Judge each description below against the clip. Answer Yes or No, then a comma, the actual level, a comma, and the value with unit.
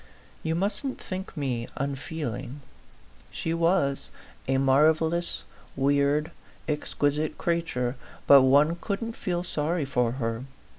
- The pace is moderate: No, slow, 115 wpm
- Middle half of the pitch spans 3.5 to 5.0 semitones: Yes, average, 3.8 semitones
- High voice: No, medium, 150 Hz